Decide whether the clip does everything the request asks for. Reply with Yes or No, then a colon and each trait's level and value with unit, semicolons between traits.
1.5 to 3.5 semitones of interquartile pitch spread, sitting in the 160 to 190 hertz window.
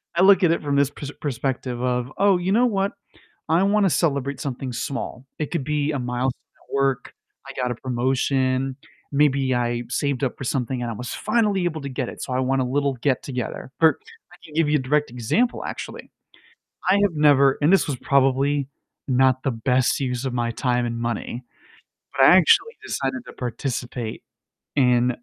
No: average, 3.2 semitones; low, 135 Hz